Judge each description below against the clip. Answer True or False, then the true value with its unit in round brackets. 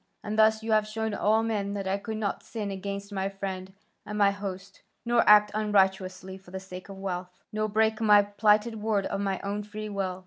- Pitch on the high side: True (205 Hz)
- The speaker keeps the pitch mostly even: True (1.8 semitones)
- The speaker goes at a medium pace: False (210 wpm)